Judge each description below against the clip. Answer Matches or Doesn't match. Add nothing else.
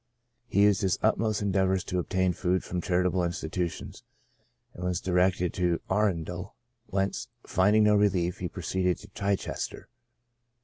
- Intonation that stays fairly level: Matches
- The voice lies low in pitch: Matches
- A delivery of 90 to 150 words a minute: Matches